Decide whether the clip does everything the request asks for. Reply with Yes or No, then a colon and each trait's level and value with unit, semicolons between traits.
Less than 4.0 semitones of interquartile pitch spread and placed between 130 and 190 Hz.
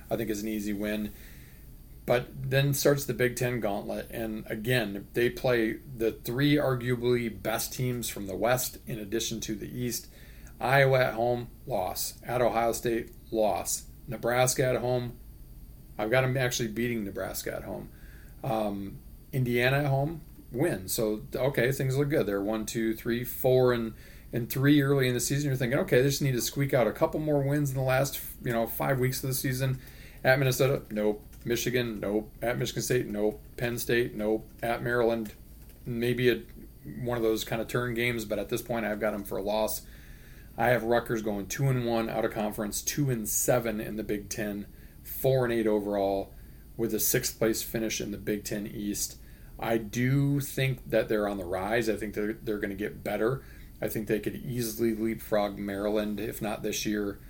No: average, 2.9 semitones; low, 115 Hz